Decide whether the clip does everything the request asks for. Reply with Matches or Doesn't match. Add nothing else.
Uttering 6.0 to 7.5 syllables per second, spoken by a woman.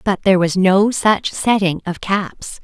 Doesn't match